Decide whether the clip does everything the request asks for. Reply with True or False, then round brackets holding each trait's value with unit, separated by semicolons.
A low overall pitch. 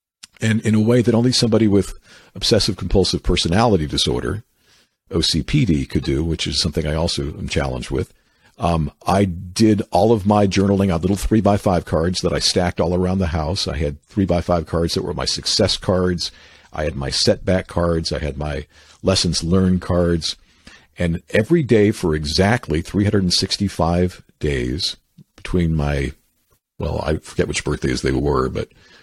True (90 Hz)